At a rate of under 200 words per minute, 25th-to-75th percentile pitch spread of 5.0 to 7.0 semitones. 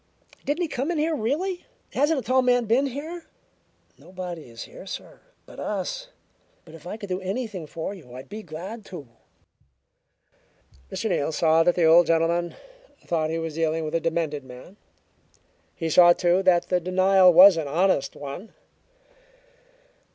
Yes: average, 165 wpm; wide, 5.6 semitones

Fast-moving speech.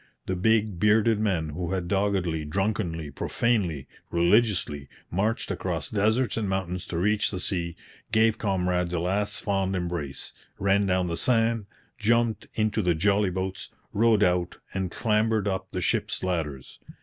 No: average, 150 wpm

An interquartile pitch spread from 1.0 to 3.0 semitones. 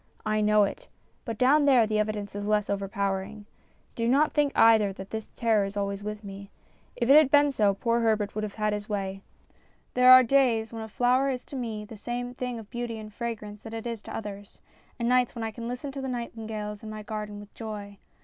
Yes: average, 2.7 semitones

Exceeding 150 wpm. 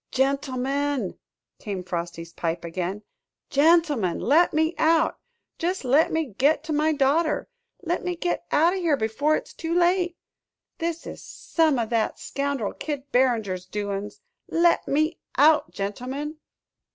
No: average, 140 wpm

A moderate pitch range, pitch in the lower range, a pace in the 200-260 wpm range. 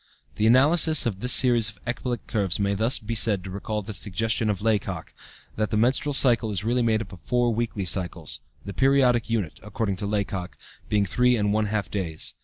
Yes: average, 3.1 semitones; low, 110 Hz; fast, 205 wpm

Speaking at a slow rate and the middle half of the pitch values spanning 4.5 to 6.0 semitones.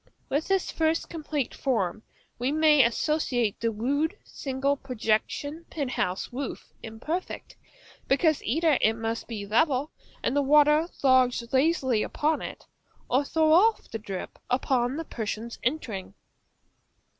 Yes: slow, 130 wpm; average, 5.1 semitones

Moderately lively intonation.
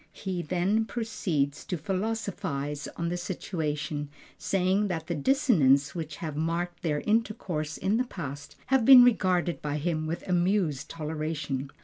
Yes: average, 4.7 semitones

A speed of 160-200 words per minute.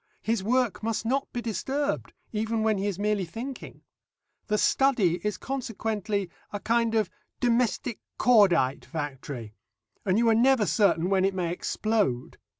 No: average, 150 wpm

